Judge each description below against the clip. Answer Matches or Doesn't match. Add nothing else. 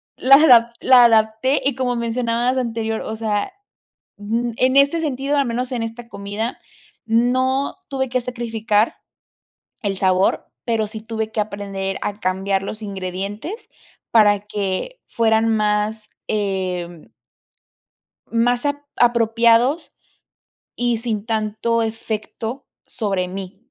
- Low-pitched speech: Doesn't match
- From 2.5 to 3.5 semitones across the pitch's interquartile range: Matches